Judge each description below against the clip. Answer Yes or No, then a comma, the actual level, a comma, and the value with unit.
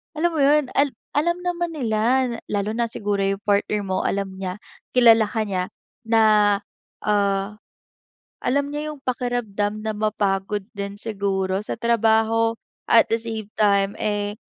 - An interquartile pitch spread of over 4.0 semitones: No, average, 3.4 semitones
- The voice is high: Yes, high, 215 Hz